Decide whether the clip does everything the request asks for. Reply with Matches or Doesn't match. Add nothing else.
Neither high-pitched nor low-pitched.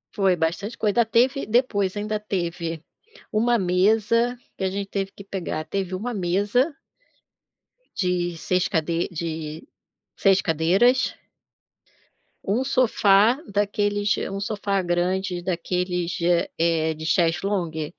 Doesn't match